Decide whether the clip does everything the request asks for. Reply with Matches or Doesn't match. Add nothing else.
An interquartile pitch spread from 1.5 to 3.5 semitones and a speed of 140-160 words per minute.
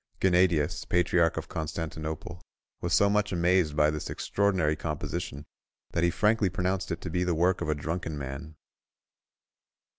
Matches